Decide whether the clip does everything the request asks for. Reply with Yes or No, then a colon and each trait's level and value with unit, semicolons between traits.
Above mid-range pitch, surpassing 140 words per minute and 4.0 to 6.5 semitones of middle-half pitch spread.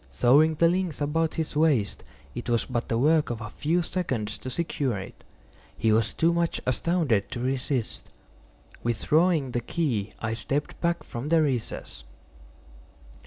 No: medium, 140 Hz; average, 155 wpm; wide, 5.6 semitones